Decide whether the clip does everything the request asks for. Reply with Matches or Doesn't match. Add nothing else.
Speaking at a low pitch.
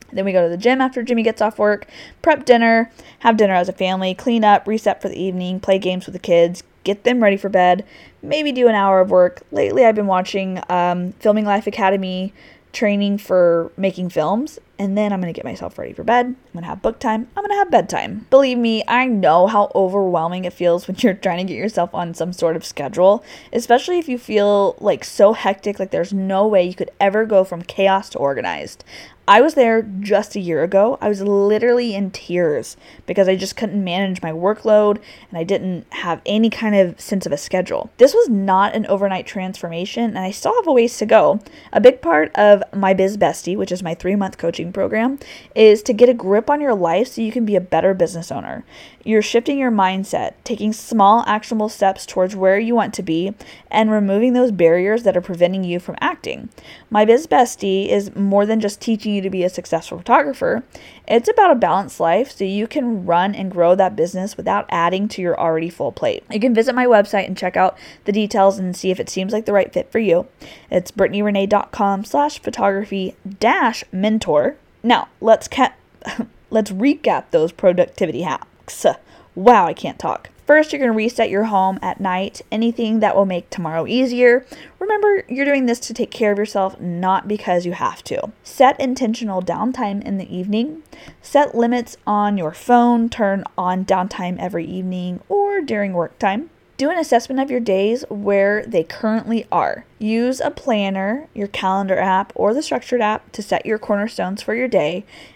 Doesn't match